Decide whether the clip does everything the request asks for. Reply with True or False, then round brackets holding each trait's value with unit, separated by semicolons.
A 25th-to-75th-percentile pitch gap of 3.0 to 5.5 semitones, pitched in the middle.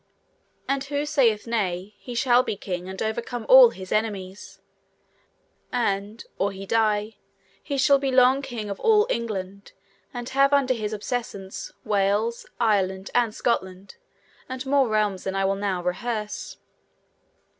False (4.4 semitones; 220 Hz)